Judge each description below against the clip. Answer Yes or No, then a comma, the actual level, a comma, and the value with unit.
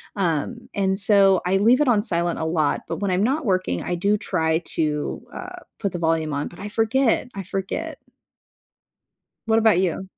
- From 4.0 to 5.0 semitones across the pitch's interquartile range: Yes, average, 4.6 semitones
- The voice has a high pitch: Yes, high, 195 Hz